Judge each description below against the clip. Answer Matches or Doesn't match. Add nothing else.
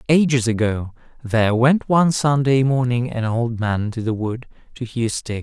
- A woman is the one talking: Doesn't match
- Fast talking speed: Doesn't match